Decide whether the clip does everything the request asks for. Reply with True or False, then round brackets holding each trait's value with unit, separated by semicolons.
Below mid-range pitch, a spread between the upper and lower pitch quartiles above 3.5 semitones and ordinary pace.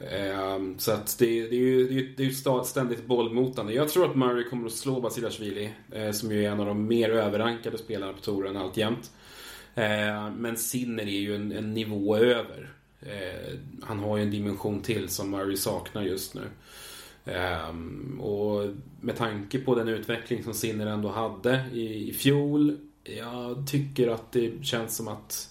False (115 Hz; 2.9 semitones; 165 wpm)